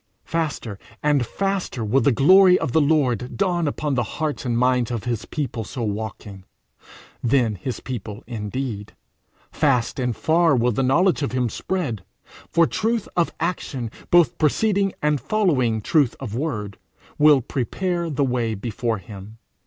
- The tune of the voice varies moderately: No, wide, 5.8 semitones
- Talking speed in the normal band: Yes, average, 155 wpm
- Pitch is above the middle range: No, low, 130 Hz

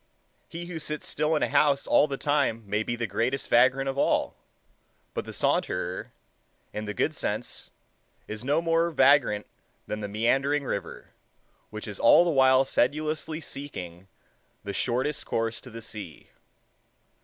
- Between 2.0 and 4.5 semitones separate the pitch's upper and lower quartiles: No, average, 5.3 semitones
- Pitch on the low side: Yes, low, 130 Hz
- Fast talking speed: No, average, 155 wpm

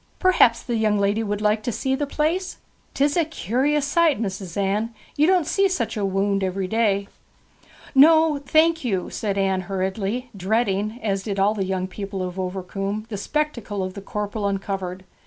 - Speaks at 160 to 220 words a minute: Yes, average, 175 wpm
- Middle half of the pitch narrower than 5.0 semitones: No, wide, 5.5 semitones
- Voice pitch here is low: No, high, 210 Hz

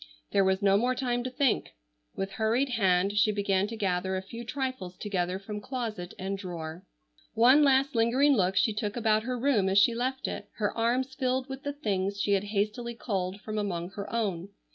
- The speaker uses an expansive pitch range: No, average, 4.3 semitones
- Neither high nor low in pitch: No, high, 210 Hz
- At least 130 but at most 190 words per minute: No, average, 200 wpm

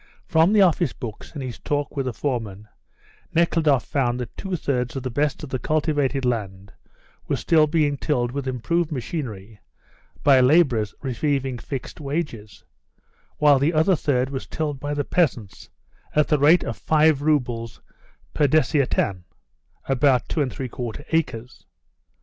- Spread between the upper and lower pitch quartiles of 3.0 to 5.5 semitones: Yes, average, 3.7 semitones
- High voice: No, medium, 140 Hz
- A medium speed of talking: Yes, average, 155 wpm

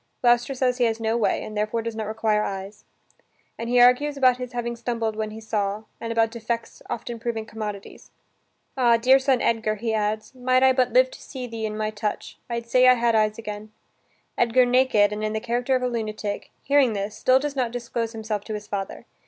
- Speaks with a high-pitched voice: Yes, high, 230 Hz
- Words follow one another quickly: Yes, fast, 215 wpm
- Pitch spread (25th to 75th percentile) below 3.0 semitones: Yes, narrow, 2.5 semitones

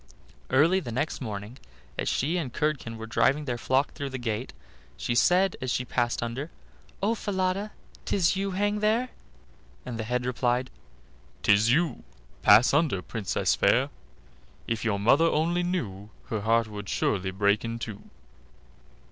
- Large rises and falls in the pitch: Yes, wide, 6.9 semitones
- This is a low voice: Yes, low, 125 Hz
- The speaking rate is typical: Yes, average, 150 wpm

